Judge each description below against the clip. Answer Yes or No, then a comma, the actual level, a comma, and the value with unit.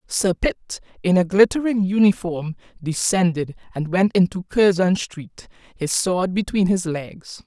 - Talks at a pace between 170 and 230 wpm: No, slow, 135 wpm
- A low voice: No, medium, 180 Hz